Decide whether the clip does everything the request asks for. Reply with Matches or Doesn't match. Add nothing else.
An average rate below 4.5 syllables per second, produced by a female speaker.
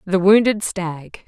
Matches